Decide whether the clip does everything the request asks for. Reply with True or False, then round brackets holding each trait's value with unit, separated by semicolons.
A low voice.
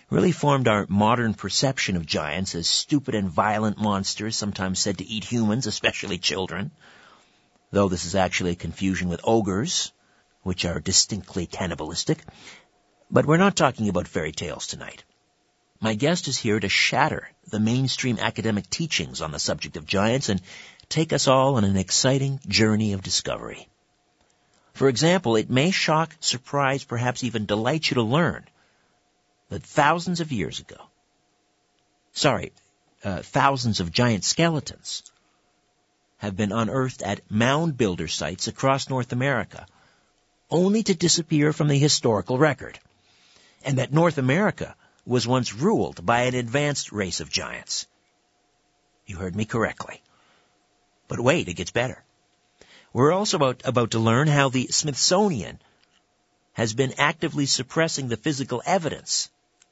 True (115 Hz)